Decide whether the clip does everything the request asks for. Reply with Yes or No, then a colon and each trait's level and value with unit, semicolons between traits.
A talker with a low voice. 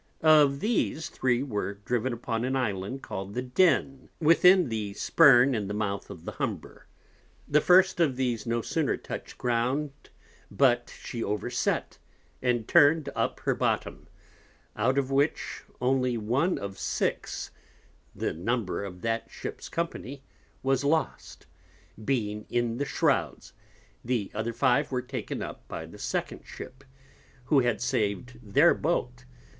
Yes: low, 125 Hz